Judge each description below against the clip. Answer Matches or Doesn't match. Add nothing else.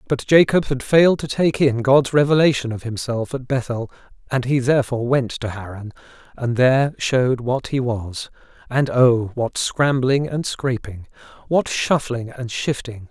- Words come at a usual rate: Matches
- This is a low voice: Matches